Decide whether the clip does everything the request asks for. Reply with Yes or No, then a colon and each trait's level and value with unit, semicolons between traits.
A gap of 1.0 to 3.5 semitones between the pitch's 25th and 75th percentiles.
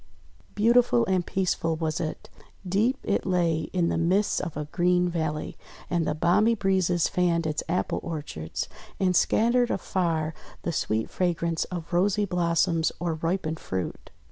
Yes: narrow, 2.6 semitones